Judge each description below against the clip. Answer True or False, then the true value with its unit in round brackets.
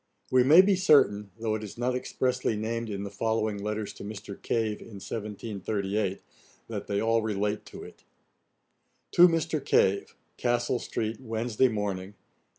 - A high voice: False (110 Hz)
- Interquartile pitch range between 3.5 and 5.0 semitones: False (2.8 semitones)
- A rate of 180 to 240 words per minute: False (155 wpm)